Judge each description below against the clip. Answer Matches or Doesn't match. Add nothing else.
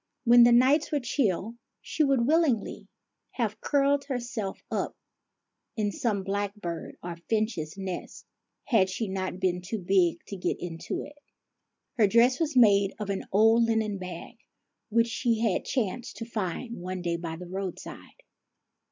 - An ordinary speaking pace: Matches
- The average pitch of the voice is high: Matches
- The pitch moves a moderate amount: Matches